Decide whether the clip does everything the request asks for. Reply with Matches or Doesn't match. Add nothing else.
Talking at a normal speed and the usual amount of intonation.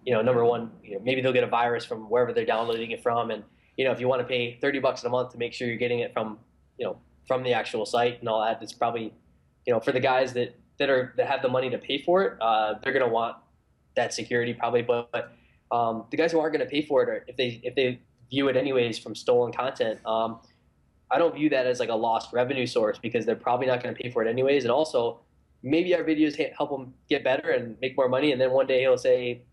Doesn't match